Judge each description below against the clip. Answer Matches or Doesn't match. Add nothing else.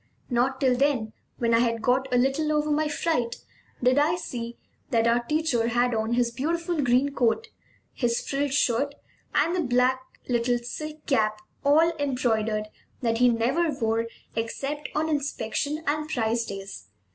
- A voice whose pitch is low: Doesn't match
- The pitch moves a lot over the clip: Doesn't match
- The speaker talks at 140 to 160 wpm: Matches